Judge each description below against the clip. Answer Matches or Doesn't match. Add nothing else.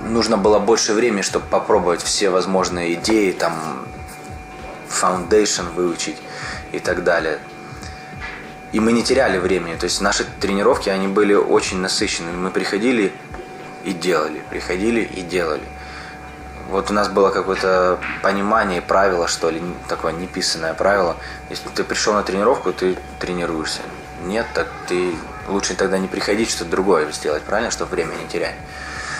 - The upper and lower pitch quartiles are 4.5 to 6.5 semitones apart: Doesn't match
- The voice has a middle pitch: Doesn't match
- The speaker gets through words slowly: Doesn't match